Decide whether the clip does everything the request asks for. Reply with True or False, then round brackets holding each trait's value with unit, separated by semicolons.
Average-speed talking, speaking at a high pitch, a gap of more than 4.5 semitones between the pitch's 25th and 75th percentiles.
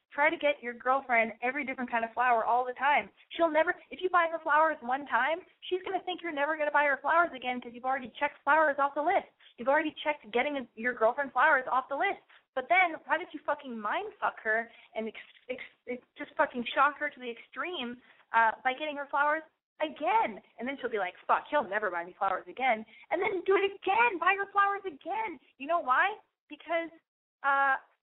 False (225 wpm; 290 Hz; 5.1 semitones)